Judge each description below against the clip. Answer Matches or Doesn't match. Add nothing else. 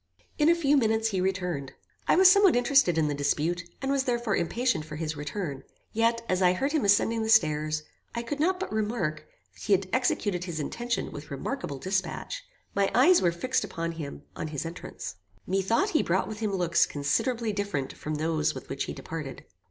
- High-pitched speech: Matches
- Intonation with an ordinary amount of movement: Doesn't match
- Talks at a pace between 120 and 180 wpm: Doesn't match